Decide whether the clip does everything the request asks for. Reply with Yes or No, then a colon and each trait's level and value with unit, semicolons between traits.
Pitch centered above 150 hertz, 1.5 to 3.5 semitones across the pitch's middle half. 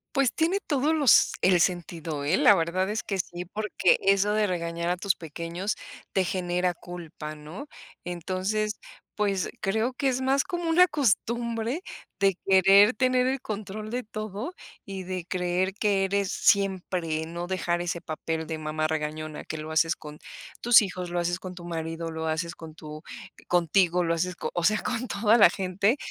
No: medium, 185 Hz; average, 4.1 semitones